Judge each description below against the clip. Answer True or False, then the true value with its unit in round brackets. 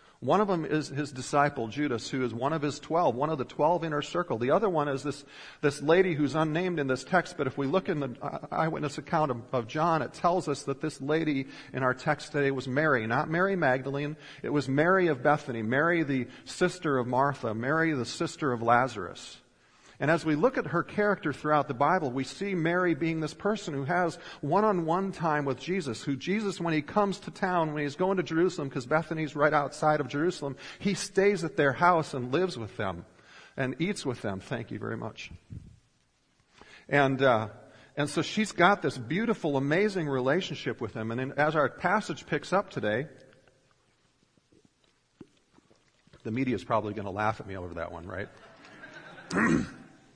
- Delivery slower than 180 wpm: False (195 wpm)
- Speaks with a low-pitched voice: False (150 Hz)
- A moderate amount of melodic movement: True (4.5 semitones)